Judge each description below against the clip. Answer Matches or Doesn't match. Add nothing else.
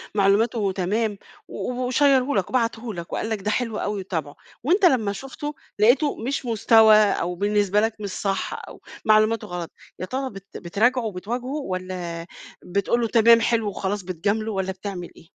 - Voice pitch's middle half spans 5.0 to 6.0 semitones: Doesn't match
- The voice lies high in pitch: Matches